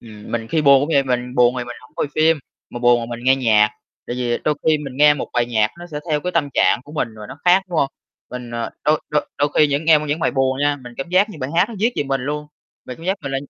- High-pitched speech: No, medium, 140 Hz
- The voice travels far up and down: No, average, 3.9 semitones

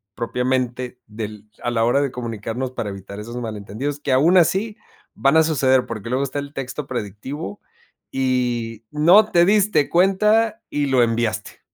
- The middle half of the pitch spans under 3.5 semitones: No, average, 4.6 semitones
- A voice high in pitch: No, low, 130 Hz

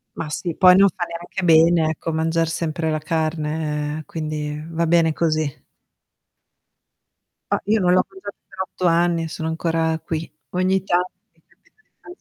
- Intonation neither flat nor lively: No, narrow, 1.8 semitones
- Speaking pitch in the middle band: Yes, medium, 165 Hz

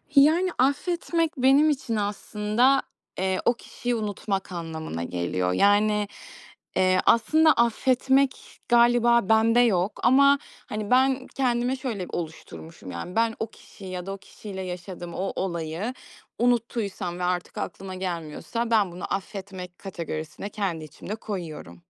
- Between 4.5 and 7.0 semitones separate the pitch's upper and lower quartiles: Yes, average, 5.2 semitones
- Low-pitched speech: No, high, 205 Hz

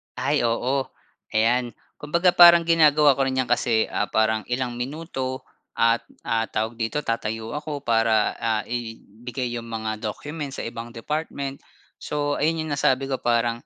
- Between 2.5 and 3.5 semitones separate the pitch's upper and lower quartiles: No, average, 4.1 semitones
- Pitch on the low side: Yes, low, 125 Hz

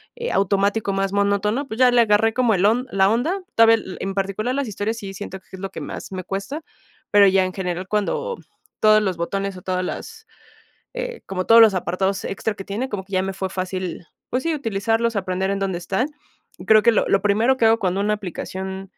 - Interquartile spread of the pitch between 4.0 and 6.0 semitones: No, average, 3.0 semitones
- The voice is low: No, high, 200 Hz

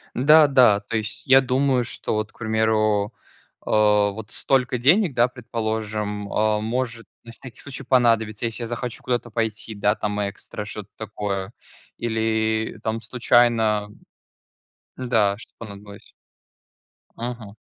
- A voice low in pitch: Yes, low, 110 Hz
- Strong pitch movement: No, narrow, 2.4 semitones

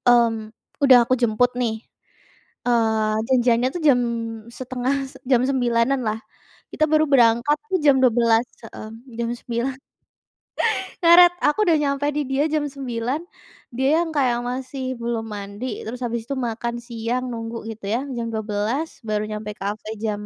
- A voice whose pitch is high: Yes, high, 240 Hz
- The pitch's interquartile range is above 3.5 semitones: No, average, 3.1 semitones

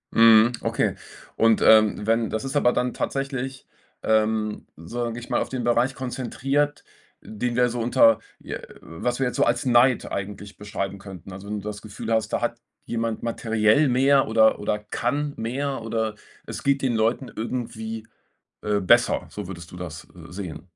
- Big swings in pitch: No, average, 2.8 semitones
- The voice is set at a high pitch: No, low, 115 Hz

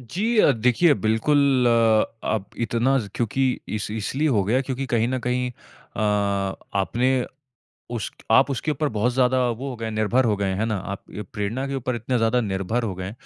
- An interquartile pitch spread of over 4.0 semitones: No, average, 3.2 semitones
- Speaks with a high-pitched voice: No, low, 120 Hz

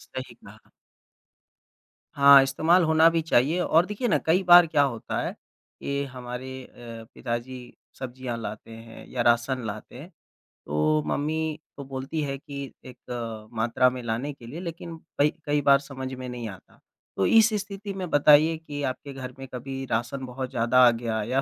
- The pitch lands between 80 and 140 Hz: Yes, low, 135 Hz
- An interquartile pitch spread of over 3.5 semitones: Yes, average, 4.2 semitones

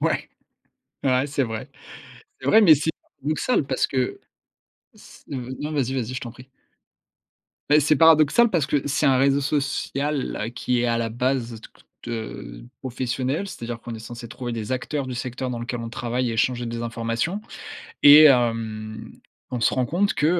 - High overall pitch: No, low, 125 Hz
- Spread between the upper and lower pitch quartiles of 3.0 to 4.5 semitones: Yes, average, 3.5 semitones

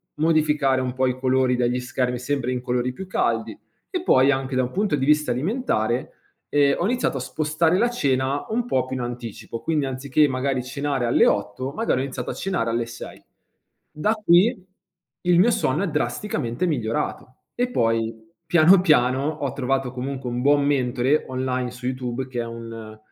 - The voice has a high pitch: No, low, 130 Hz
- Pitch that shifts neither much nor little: Yes, average, 3.6 semitones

